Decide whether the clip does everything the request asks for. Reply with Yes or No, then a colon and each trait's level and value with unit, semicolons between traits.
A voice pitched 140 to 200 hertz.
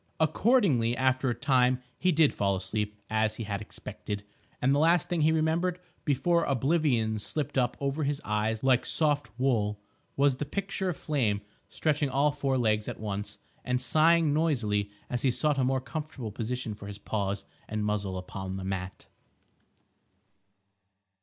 No: low, 130 Hz